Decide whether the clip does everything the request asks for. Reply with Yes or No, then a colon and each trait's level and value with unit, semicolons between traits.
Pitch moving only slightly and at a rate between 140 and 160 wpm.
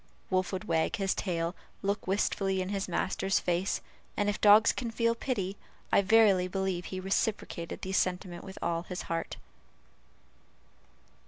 Yes: narrow, 2.0 semitones; average, 150 wpm